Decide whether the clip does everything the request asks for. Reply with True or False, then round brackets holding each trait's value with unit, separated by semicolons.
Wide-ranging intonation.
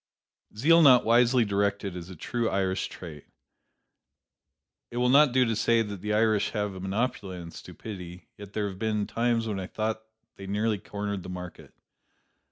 False (3.2 semitones)